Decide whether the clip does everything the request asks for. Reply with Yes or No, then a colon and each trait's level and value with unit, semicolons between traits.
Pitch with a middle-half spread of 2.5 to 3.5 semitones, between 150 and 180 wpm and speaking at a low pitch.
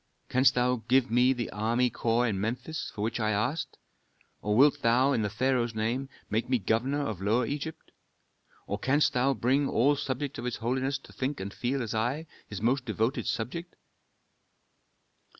Yes: average, 3.1 semitones; average, 175 wpm; low, 125 Hz